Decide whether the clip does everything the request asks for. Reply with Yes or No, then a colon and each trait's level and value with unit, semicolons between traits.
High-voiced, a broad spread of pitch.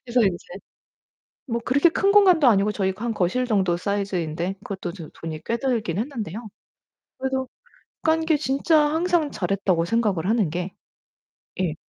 Yes: high, 215 Hz; wide, 6.4 semitones